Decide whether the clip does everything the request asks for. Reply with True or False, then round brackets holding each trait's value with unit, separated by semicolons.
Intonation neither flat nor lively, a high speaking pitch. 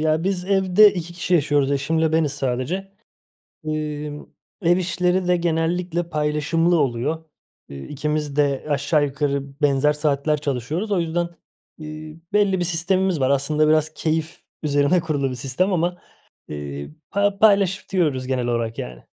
False (3.8 semitones; 155 Hz)